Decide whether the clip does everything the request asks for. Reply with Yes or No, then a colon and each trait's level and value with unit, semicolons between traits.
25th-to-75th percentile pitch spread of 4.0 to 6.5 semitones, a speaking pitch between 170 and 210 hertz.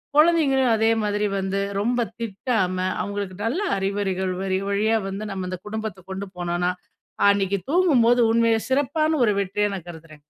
No: average, 3.5 semitones; high, 205 Hz